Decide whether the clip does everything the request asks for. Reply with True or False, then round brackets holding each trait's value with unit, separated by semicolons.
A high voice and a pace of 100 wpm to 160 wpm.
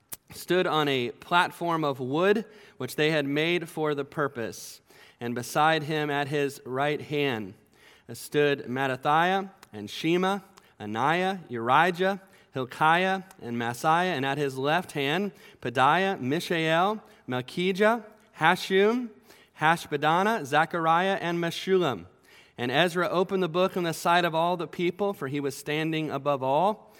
False (160 Hz; 135 wpm)